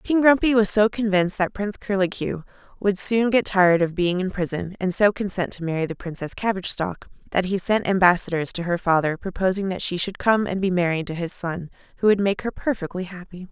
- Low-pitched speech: No, high, 190 Hz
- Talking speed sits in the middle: No, fast, 220 wpm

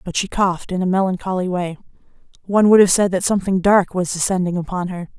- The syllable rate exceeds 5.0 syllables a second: Yes, 6.5 syllables/s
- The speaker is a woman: Yes, female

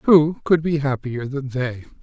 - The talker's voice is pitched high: No, medium, 140 Hz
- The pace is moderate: Yes, average, 175 wpm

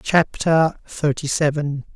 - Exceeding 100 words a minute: No, slow, 90 wpm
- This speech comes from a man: Yes, male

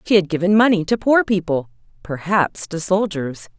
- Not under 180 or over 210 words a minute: No, average, 165 wpm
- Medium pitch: Yes, medium, 180 Hz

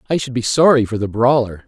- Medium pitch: No, low, 120 Hz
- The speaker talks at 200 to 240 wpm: No, fast, 250 wpm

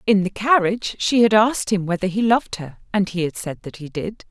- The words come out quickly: Yes, fast, 250 wpm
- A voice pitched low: No, high, 200 Hz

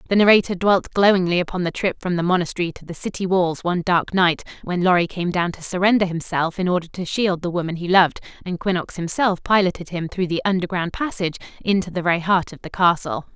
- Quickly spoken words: Yes, fast, 215 wpm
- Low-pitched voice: No, medium, 180 Hz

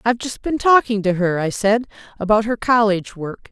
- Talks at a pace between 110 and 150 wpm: No, fast, 205 wpm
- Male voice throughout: No, female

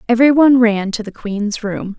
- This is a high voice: Yes, high, 225 Hz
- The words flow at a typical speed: No, fast, 210 wpm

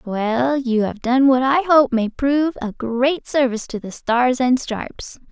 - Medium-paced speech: Yes, average, 190 wpm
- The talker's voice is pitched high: Yes, very high, 255 Hz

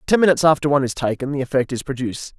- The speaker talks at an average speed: No, fast, 250 wpm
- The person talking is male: Yes, male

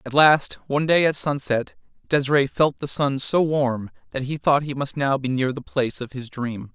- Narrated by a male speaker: Yes, male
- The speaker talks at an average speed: No, fast, 220 wpm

